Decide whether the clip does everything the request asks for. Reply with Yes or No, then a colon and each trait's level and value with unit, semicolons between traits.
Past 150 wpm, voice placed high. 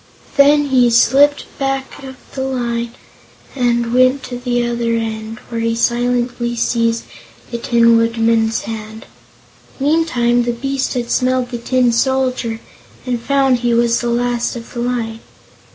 No: average, 145 wpm; high, 240 Hz